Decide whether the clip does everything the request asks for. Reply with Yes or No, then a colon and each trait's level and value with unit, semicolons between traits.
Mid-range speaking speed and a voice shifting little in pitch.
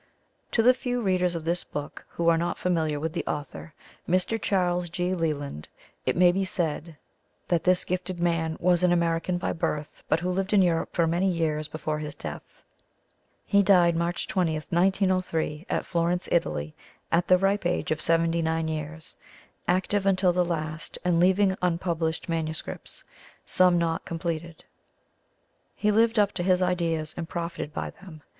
Yes: average, 165 wpm; narrow, 2.1 semitones